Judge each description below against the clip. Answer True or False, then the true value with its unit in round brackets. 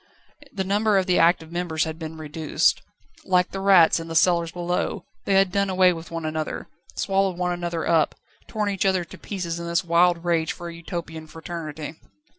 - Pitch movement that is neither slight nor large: False (2.3 semitones)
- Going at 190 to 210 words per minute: True (195 wpm)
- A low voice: False (170 Hz)